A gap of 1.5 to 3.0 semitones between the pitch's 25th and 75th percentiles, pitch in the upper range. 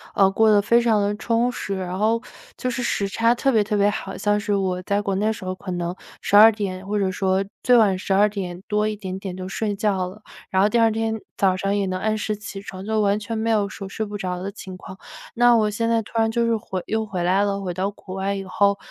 Yes: narrow, 2.4 semitones; high, 205 Hz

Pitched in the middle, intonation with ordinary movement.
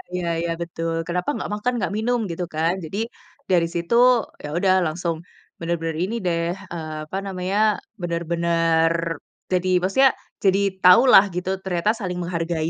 No: medium, 175 Hz; narrow, 2.0 semitones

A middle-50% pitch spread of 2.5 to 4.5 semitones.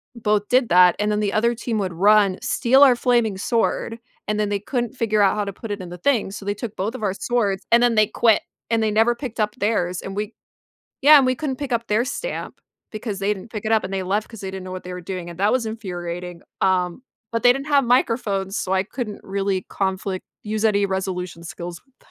Yes: average, 3.6 semitones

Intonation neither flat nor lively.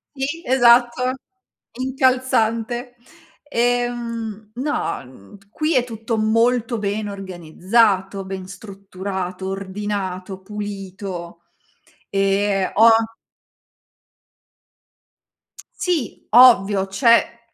Yes: average, 3.9 semitones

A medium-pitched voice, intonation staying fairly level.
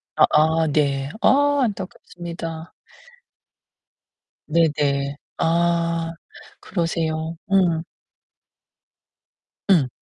Yes: medium, 165 Hz; narrow, 1.5 semitones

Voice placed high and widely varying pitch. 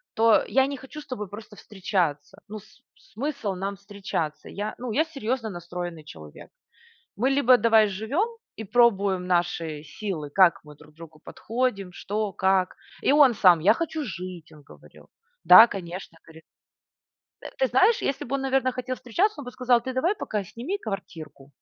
Yes: high, 210 Hz; wide, 6.1 semitones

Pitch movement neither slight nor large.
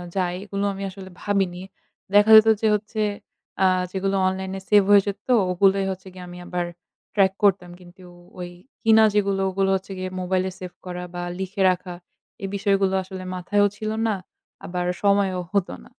No: narrow, 1.5 semitones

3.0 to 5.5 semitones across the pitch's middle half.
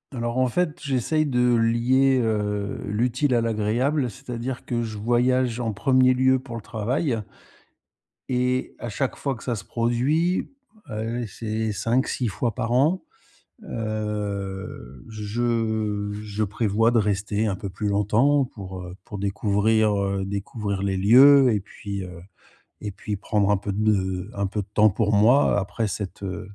Yes: average, 3.4 semitones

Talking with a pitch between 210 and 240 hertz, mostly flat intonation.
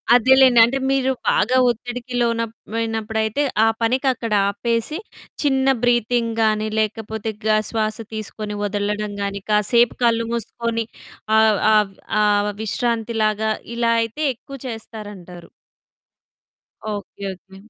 Yes: high, 225 Hz; narrow, 2.2 semitones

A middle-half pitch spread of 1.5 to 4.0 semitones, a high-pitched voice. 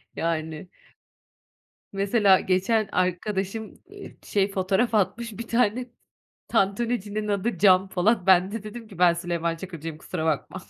Yes: average, 3.4 semitones; high, 195 Hz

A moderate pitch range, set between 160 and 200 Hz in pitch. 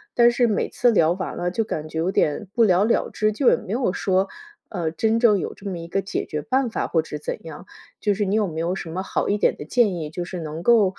Yes: average, 4.7 semitones; high, 190 Hz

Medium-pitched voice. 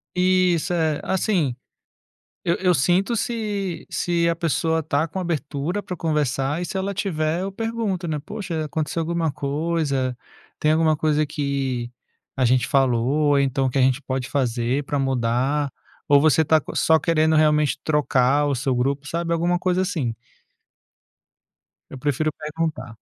Yes: medium, 155 Hz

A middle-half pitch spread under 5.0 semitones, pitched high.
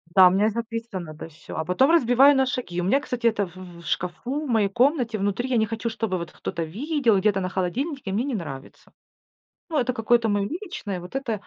No: wide, 5.4 semitones; high, 220 Hz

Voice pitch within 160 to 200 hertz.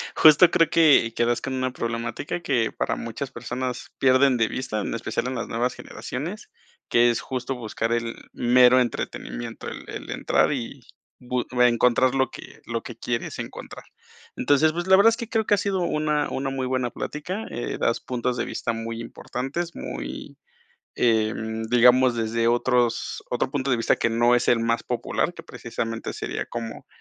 No: low, 125 Hz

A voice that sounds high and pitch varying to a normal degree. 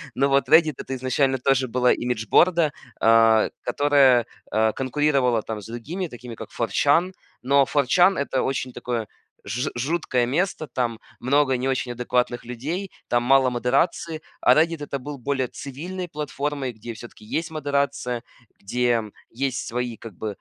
No: low, 130 Hz; average, 3.3 semitones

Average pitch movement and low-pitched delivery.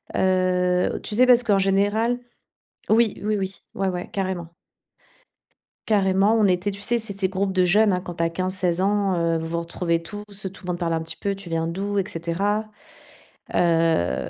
No: average, 3.0 semitones; high, 190 Hz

